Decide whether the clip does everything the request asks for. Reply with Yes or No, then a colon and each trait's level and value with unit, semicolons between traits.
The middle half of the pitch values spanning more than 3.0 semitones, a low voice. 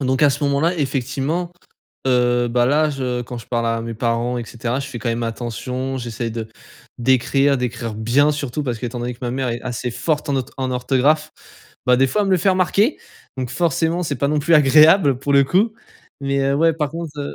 Yes: average, 3.6 semitones; low, 130 Hz